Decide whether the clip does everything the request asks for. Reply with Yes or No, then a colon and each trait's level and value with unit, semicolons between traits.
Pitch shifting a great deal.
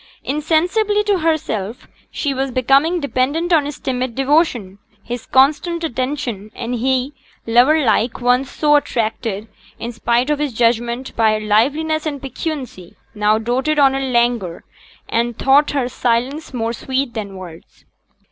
No: average, 4.2 semitones